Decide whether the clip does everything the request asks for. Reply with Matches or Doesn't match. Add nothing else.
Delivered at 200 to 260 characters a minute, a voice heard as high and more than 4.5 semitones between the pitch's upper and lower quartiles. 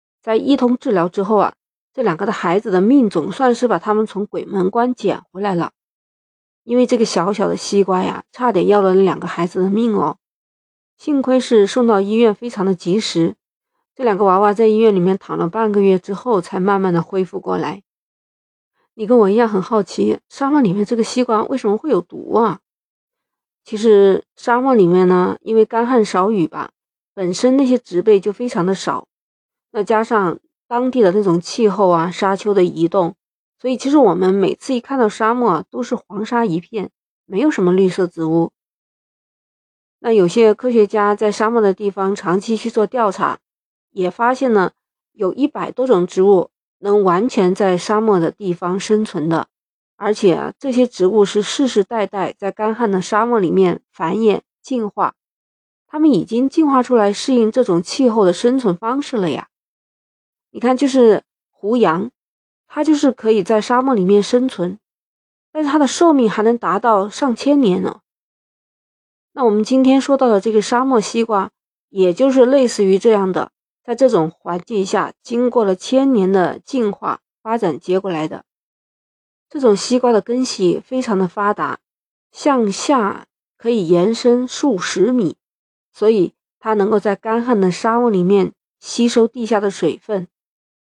Doesn't match